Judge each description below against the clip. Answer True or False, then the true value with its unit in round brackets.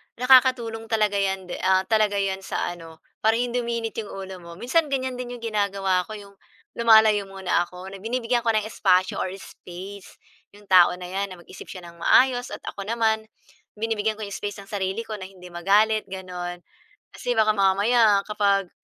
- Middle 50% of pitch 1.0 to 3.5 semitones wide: True (3.0 semitones)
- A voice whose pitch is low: False (205 Hz)